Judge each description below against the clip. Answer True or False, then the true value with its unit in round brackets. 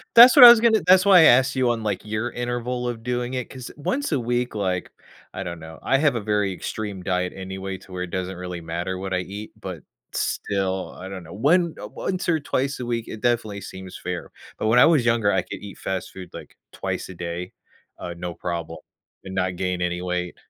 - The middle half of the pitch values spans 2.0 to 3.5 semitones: False (5.2 semitones)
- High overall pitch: False (100 Hz)